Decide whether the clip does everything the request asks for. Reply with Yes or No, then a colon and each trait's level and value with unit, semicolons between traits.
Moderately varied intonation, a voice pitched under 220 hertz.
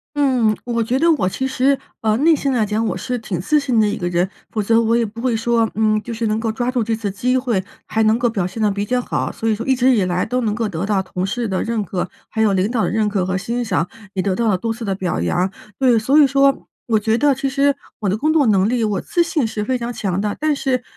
No: average, 3.6 semitones; high, 225 Hz